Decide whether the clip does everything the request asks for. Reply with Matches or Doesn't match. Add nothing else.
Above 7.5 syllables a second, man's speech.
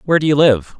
Matches